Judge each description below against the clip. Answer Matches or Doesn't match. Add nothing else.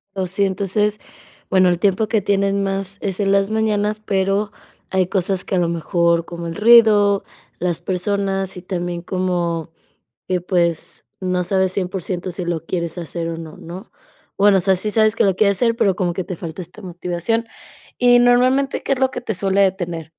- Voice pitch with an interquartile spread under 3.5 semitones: Matches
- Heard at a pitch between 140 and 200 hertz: Matches